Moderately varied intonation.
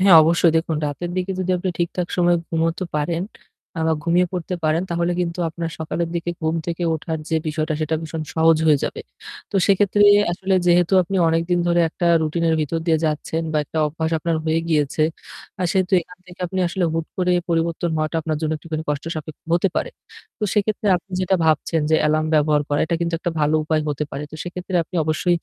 No: narrow, 2.0 semitones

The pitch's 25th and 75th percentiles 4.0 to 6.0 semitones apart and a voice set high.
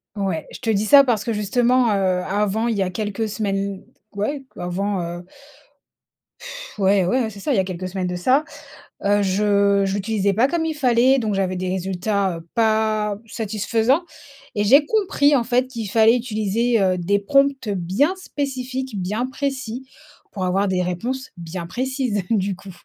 Yes: average, 4.6 semitones; high, 210 Hz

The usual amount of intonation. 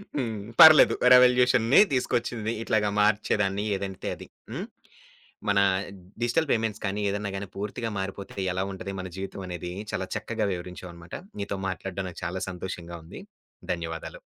Yes: average, 3.2 semitones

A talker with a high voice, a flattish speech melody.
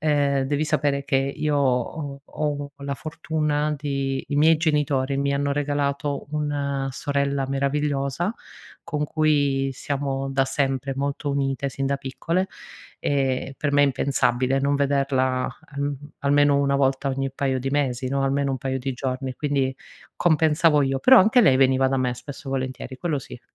No: medium, 140 Hz; narrow, 1.4 semitones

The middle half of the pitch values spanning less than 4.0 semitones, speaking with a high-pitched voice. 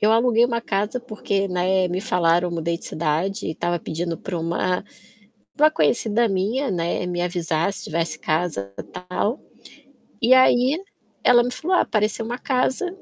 No: wide, 5.6 semitones; high, 195 Hz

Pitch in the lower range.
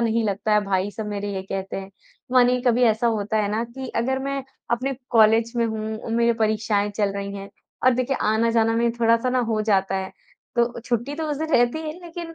No: high, 230 Hz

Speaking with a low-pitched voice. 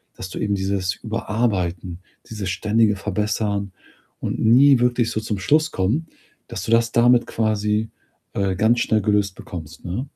Yes: low, 105 Hz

